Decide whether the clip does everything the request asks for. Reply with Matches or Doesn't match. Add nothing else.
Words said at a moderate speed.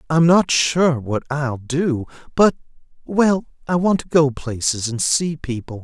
Matches